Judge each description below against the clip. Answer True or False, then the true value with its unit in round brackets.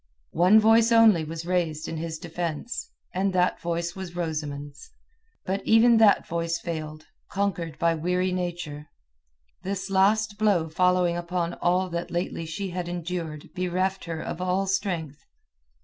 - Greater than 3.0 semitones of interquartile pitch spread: False (2.6 semitones)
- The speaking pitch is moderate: True (175 Hz)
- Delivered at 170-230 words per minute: False (145 wpm)